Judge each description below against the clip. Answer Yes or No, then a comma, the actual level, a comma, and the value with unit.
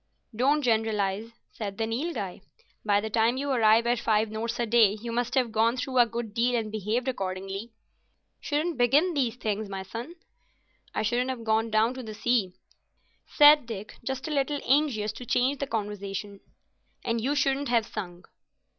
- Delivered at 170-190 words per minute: Yes, average, 175 wpm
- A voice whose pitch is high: Yes, high, 230 Hz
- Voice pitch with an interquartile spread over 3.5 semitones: No, average, 3.2 semitones